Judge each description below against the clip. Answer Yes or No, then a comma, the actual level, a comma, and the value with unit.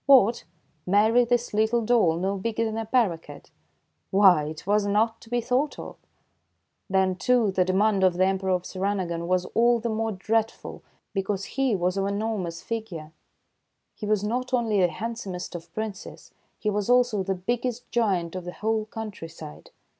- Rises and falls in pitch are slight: No, average, 3.4 semitones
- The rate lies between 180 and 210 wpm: No, average, 170 wpm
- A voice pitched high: Yes, high, 205 Hz